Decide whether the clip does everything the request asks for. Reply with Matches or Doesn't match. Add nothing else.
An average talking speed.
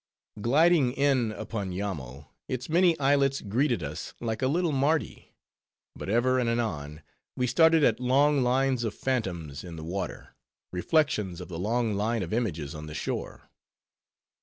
Matches